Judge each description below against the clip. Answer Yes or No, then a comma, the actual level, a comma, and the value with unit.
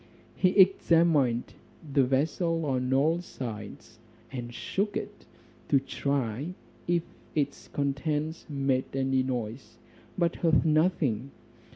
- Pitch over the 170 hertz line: No, medium, 140 Hz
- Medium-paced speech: No, slow, 105 wpm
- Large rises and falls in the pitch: No, average, 4.1 semitones